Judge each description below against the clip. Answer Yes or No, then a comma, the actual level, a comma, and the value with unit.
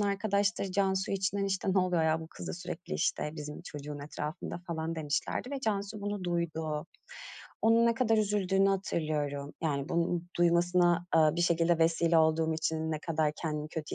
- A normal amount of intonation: Yes, average, 3.6 semitones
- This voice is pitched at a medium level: Yes, medium, 170 Hz